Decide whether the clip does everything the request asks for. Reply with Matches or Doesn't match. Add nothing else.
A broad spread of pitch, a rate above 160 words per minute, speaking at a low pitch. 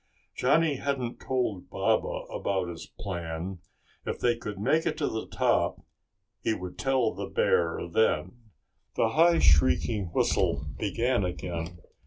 Doesn't match